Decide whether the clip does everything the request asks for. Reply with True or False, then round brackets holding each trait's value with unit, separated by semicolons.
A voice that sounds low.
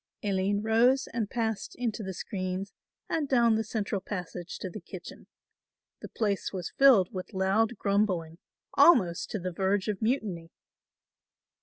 False (200 Hz)